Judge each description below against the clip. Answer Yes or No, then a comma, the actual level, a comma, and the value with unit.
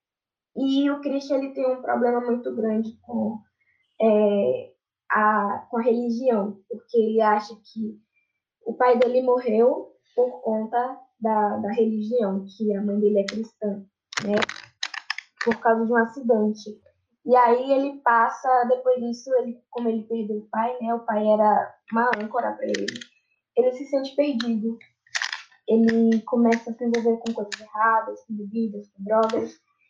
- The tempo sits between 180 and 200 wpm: No, average, 155 wpm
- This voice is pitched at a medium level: No, high, 230 Hz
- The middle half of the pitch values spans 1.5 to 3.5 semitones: Yes, narrow, 2.4 semitones